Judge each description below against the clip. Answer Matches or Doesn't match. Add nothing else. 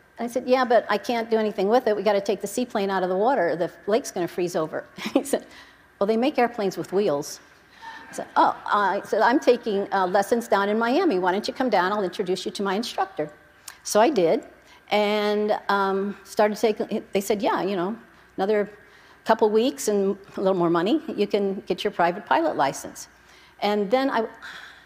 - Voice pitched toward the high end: Matches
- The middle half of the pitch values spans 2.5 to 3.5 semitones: Matches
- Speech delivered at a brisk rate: Matches